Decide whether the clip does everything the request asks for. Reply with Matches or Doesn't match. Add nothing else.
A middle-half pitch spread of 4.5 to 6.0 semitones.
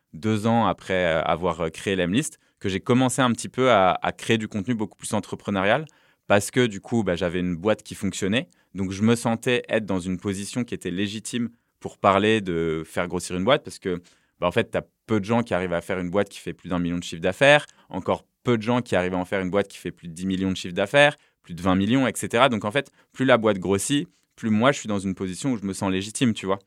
Doesn't match